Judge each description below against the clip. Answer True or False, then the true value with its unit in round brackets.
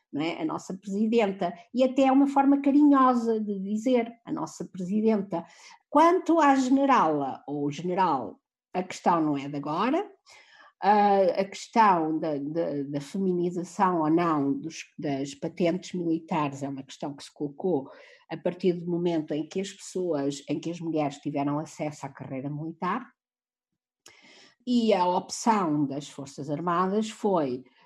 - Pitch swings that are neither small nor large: False (6.7 semitones)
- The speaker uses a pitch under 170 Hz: False (175 Hz)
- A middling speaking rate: True (140 wpm)